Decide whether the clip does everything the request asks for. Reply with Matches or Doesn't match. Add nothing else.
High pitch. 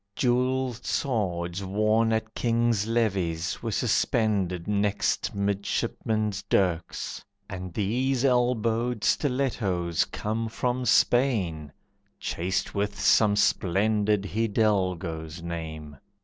Doesn't match